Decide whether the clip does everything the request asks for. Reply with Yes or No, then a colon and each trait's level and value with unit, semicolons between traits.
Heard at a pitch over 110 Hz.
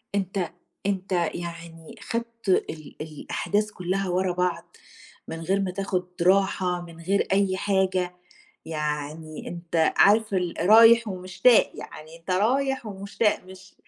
Yes: medium, 185 Hz